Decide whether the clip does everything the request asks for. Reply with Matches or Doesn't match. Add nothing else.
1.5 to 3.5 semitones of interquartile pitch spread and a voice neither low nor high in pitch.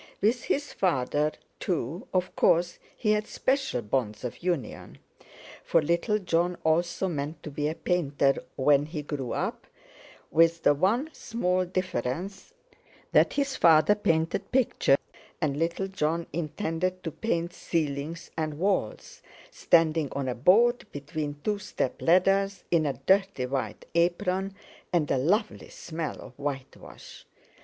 Doesn't match